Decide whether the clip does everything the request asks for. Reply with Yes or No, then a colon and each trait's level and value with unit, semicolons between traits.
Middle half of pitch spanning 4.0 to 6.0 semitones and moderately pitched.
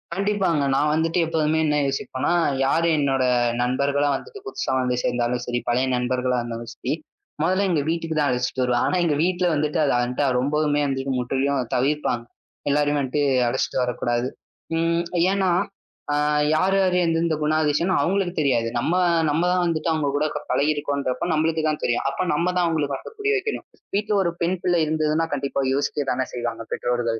Yes: average, 4.3 semitones; medium, 145 Hz